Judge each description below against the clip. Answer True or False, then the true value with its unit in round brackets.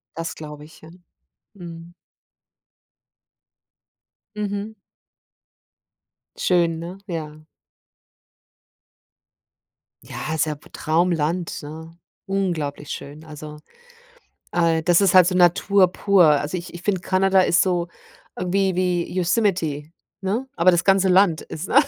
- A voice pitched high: False (175 Hz)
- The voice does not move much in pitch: False (3.0 semitones)